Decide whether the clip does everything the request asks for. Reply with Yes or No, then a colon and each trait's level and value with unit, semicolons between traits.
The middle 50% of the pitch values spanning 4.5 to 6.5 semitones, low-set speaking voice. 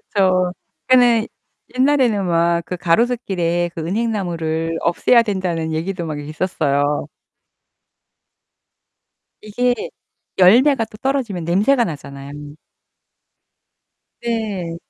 No: wide, 5.6 semitones; medium, 185 Hz